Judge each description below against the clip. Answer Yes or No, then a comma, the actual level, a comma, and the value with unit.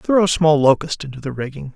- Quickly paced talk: Yes, fast, 240 wpm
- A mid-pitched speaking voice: Yes, medium, 150 Hz